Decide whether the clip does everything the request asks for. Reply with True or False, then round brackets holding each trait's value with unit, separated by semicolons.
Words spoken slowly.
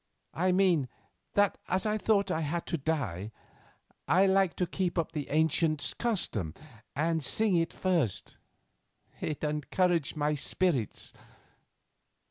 True (125 wpm)